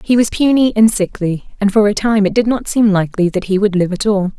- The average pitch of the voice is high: Yes, high, 205 Hz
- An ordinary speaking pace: No, fast, 275 wpm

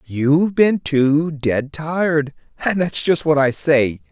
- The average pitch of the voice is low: No, medium, 150 Hz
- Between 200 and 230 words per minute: No, average, 160 wpm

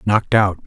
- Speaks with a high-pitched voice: No, low, 100 Hz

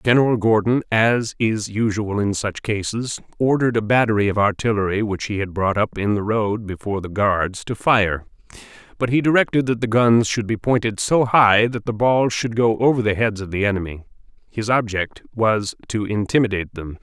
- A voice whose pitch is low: Yes, low, 110 Hz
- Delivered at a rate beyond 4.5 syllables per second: Yes, 5.2 syllables/s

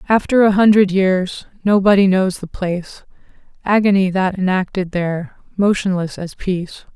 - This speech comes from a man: No, female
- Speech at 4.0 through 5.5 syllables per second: Yes, 4.9 syllables/s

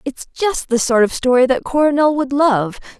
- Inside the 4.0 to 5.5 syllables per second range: Yes, 4.9 syllables/s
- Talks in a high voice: Yes, very high, 265 Hz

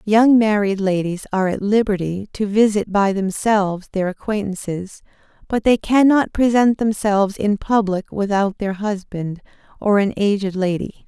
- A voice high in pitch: Yes, high, 205 Hz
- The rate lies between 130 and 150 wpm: Yes, average, 140 wpm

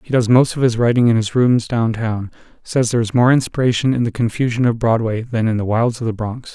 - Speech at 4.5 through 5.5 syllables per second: No, 5.7 syllables/s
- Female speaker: No, male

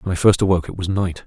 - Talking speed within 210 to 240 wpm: No, fast, 330 wpm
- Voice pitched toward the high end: No, very low, 95 Hz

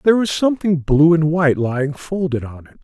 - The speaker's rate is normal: No, fast, 210 wpm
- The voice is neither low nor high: Yes, medium, 160 Hz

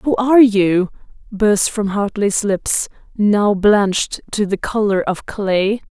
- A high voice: Yes, high, 205 Hz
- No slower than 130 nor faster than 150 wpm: Yes, average, 140 wpm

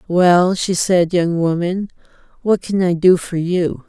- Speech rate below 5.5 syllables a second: Yes, 3.8 syllables/s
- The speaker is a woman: Yes, female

